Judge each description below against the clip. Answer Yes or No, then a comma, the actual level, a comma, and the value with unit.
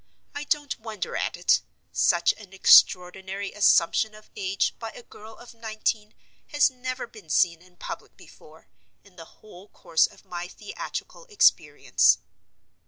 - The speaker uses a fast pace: No, average, 145 wpm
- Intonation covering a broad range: No, average, 4.3 semitones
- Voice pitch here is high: Yes, high, 210 Hz